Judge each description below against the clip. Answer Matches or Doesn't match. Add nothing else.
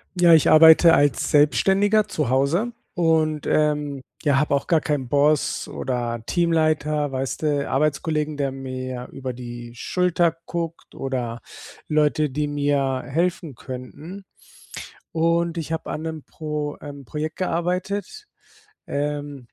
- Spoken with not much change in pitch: Doesn't match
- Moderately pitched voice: Matches